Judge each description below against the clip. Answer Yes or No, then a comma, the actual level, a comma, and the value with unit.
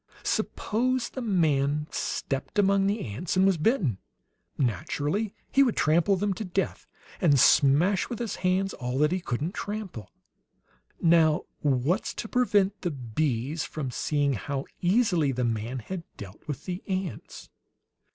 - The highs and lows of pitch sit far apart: Yes, wide, 6.2 semitones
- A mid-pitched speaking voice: Yes, medium, 170 Hz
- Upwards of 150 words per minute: No, average, 145 wpm